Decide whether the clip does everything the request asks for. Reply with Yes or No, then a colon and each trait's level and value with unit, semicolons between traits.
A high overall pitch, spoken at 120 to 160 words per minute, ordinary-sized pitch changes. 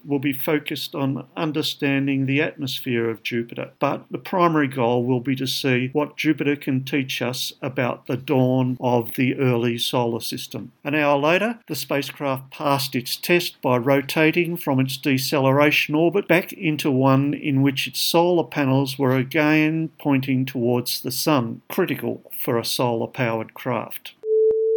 No: medium, 140 Hz; average, 155 wpm; average, 3.1 semitones